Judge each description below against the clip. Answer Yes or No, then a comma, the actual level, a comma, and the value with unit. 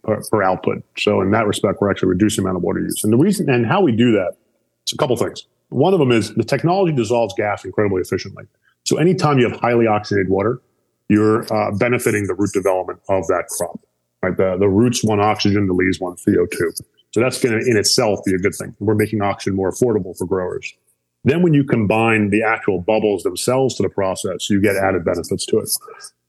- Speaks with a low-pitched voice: Yes, low, 110 Hz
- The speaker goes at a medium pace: No, fast, 220 wpm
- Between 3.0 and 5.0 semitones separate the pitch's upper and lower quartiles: Yes, average, 3.7 semitones